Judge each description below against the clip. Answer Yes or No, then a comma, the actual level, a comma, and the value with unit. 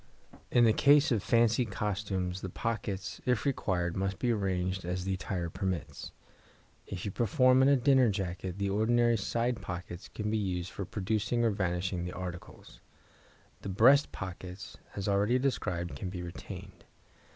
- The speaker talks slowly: No, average, 160 wpm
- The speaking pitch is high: No, low, 100 Hz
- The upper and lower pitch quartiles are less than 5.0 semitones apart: Yes, average, 4.2 semitones